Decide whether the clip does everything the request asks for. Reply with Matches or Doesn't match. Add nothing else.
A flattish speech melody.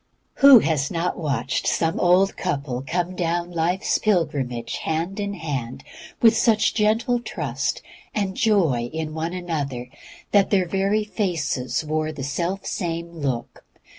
Doesn't match